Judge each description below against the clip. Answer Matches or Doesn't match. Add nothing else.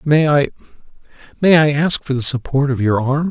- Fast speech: Doesn't match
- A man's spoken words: Matches